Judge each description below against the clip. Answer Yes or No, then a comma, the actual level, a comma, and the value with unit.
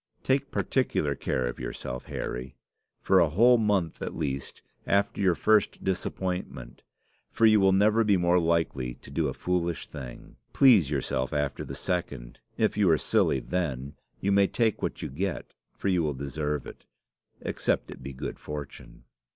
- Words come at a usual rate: Yes, average, 165 wpm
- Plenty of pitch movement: Yes, wide, 6.3 semitones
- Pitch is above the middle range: No, very low, 85 Hz